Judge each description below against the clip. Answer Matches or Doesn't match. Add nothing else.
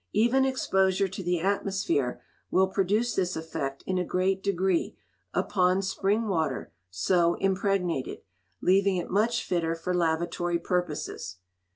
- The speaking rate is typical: Doesn't match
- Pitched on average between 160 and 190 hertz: Matches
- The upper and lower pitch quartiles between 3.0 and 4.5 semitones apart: Doesn't match